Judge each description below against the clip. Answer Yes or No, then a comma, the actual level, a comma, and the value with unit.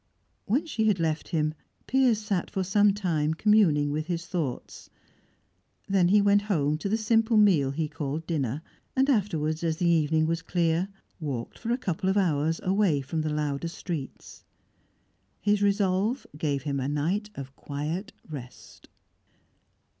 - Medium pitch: Yes, medium, 170 Hz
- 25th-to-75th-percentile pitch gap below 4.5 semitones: No, average, 5.1 semitones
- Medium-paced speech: Yes, average, 155 wpm